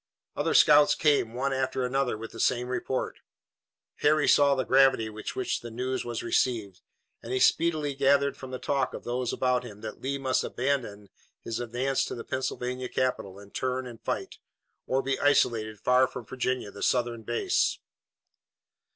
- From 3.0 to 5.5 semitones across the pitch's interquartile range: No, narrow, 2.4 semitones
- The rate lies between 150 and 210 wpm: Yes, average, 170 wpm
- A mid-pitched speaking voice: No, low, 125 Hz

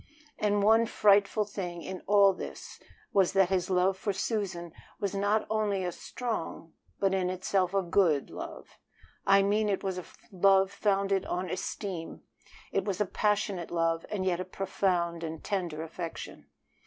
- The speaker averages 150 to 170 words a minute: Yes, average, 160 wpm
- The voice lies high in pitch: Yes, high, 195 Hz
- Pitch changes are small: Yes, narrow, 2.1 semitones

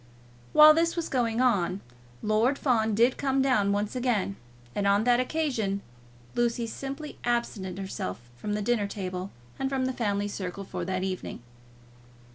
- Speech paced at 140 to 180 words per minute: Yes, average, 155 wpm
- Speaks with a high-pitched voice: Yes, high, 220 Hz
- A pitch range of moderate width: Yes, average, 4.4 semitones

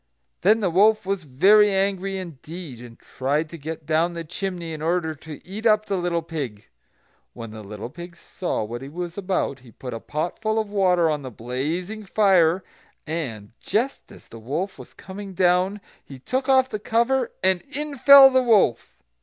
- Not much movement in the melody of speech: No, average, 5.3 semitones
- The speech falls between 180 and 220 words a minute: Yes, average, 185 wpm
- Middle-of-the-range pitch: Yes, medium, 175 Hz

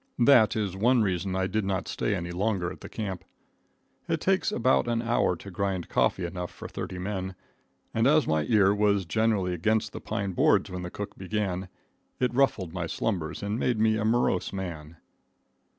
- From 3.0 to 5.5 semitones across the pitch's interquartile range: Yes, average, 3.3 semitones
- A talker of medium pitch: No, low, 100 Hz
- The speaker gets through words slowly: No, average, 185 wpm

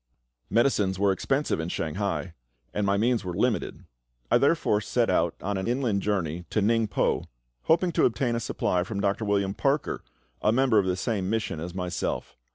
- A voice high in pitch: No, low, 100 Hz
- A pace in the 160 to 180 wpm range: Yes, average, 175 wpm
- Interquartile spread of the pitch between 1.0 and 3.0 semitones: No, average, 3.8 semitones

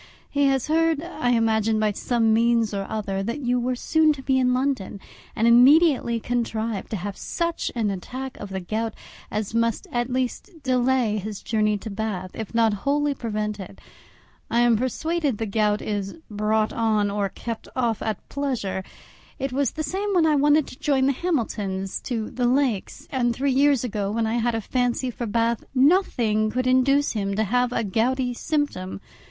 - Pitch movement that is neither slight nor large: Yes, average, 3.7 semitones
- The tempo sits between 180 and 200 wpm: Yes, average, 185 wpm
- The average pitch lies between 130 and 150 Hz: No, high, 235 Hz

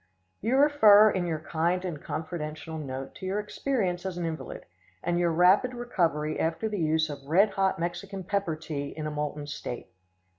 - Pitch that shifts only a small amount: No, average, 4.2 semitones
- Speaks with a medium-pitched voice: Yes, medium, 175 Hz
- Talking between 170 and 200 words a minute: Yes, average, 180 wpm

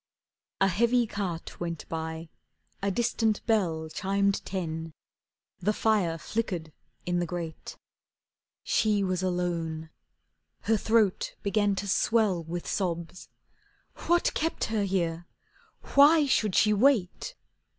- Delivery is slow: Yes, slow, 115 wpm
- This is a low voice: No, high, 190 Hz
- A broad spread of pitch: No, average, 4.4 semitones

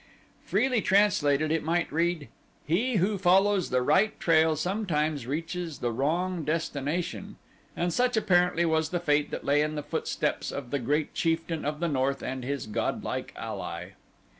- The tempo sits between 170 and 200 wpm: No, average, 160 wpm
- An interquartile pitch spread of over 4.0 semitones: No, average, 3.5 semitones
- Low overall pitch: No, medium, 160 Hz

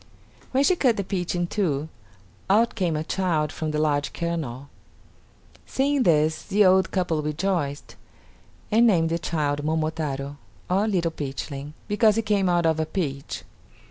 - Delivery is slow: No, average, 155 wpm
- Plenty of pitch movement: No, average, 4.5 semitones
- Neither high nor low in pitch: Yes, medium, 165 Hz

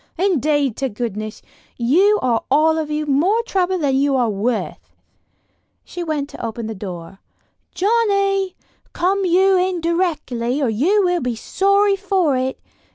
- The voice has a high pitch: Yes, very high, 310 Hz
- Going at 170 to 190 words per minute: No, average, 150 wpm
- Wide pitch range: Yes, wide, 7.2 semitones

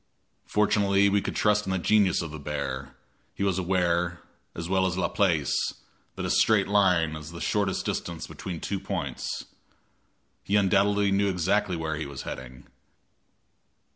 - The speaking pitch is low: Yes, very low, 95 Hz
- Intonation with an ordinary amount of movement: Yes, average, 3.3 semitones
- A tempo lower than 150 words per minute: No, average, 160 wpm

